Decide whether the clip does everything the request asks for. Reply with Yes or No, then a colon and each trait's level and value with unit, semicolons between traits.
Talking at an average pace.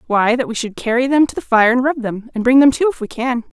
No: fast, 320 wpm